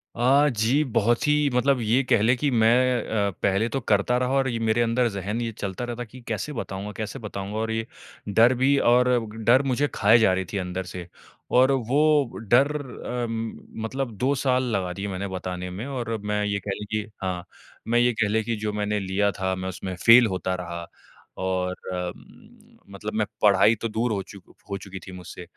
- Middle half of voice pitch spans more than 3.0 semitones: Yes, average, 4.0 semitones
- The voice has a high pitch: No, low, 110 Hz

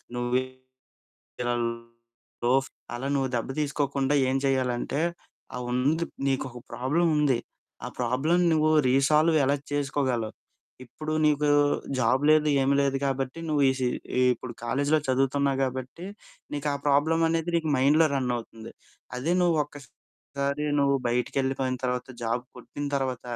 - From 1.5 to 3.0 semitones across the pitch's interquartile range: Yes, average, 2.7 semitones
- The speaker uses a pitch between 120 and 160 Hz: Yes, low, 135 Hz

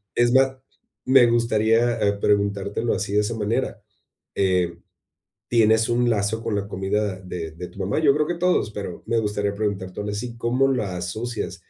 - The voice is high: No, low, 105 Hz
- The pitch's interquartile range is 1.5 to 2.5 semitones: No, average, 2.9 semitones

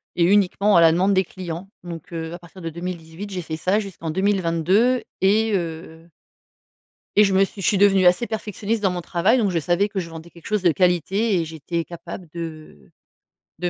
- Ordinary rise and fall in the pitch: Yes, average, 3.1 semitones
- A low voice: No, medium, 180 Hz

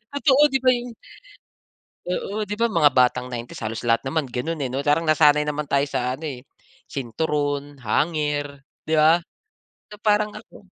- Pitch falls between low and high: Yes, medium, 150 Hz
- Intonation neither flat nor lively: Yes, average, 3.4 semitones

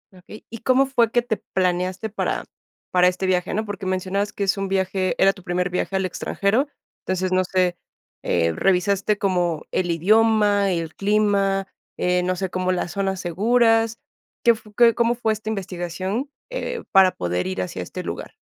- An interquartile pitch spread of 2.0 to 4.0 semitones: Yes, average, 3.1 semitones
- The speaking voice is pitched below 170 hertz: No, high, 195 Hz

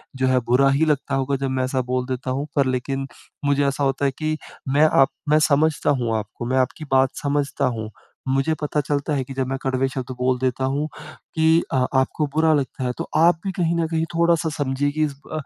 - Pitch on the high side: No, low, 135 Hz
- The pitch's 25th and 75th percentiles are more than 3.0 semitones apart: No, narrow, 2.5 semitones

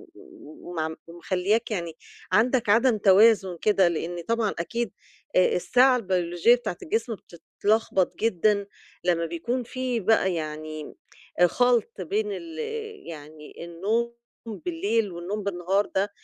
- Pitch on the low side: No, high, 200 Hz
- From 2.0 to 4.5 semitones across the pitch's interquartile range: No, average, 5.0 semitones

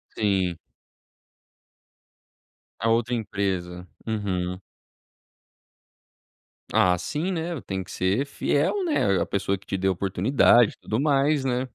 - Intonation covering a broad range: Yes, wide, 6.3 semitones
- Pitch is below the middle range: Yes, low, 105 Hz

